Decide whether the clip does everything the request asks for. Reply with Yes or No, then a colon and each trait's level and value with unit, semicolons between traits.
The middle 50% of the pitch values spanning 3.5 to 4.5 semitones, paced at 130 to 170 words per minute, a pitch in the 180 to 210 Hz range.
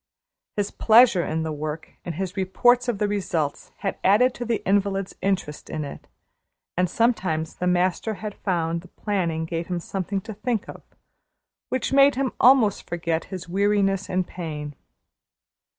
Yes: average, 3.9 semitones; average, 160 wpm; high, 190 Hz